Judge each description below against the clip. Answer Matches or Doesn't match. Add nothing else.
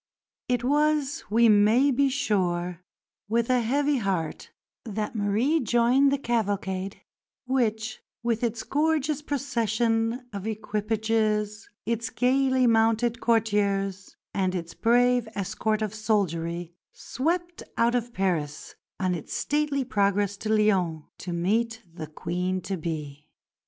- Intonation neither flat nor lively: Matches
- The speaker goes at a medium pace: Doesn't match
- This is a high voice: Matches